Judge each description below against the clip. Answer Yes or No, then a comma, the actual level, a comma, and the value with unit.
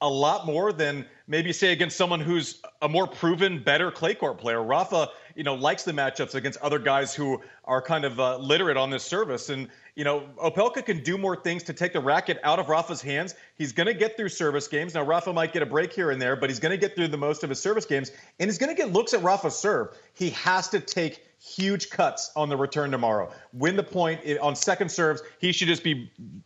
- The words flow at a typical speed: No, fast, 245 wpm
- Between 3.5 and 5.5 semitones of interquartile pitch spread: Yes, average, 4.3 semitones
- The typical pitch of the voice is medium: Yes, medium, 160 Hz